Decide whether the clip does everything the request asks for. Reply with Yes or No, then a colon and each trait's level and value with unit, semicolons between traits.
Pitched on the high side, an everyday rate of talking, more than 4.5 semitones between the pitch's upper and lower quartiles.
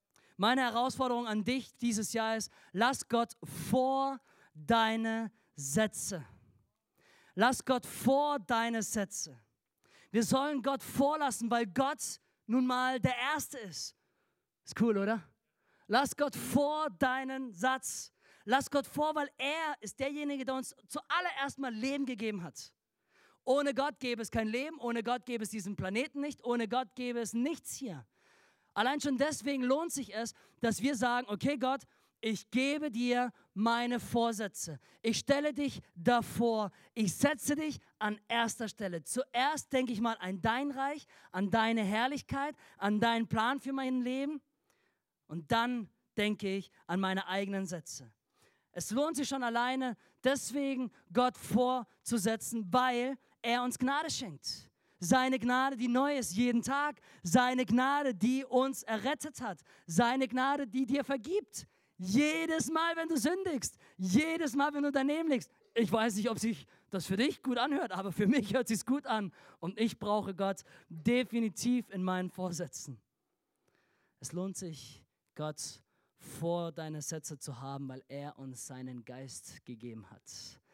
Yes: high, 240 Hz; average, 150 wpm; average, 5.0 semitones